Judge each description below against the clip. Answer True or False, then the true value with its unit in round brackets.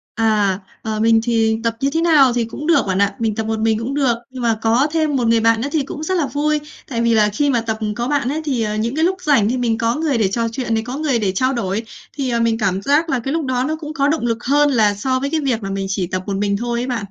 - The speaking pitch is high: True (235 Hz)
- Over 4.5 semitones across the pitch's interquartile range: False (4.2 semitones)